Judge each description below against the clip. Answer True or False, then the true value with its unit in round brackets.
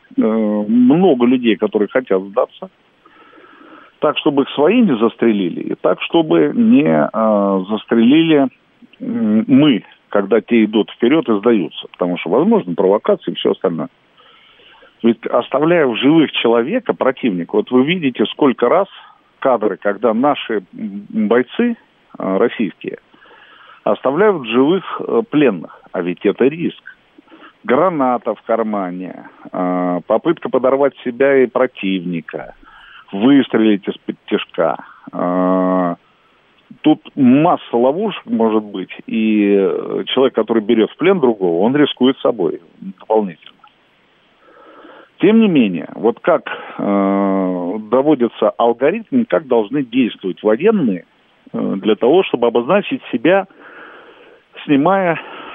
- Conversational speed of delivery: False (105 wpm)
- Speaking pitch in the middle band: False (125 Hz)